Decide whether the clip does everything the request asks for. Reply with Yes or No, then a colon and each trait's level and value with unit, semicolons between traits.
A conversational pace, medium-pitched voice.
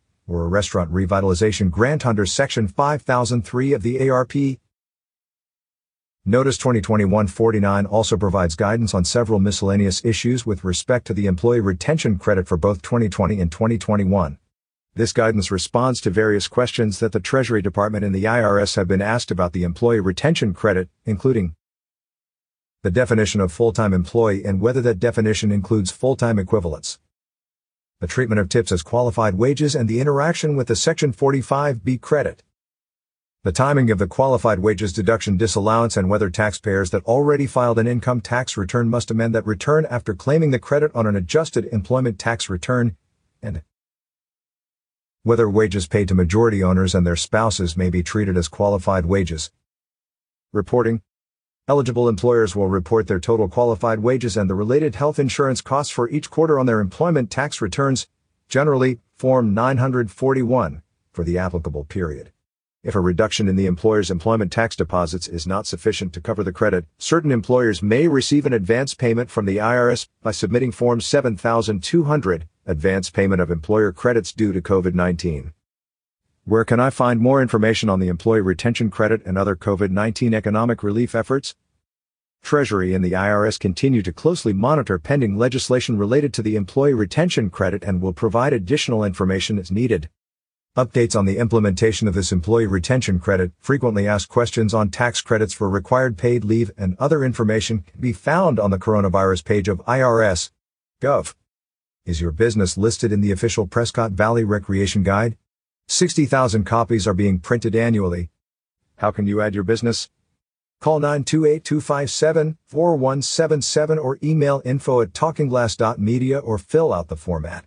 No: average, 155 wpm; low, 110 Hz